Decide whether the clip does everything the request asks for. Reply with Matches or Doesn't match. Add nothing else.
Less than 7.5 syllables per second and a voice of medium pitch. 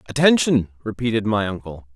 Doesn't match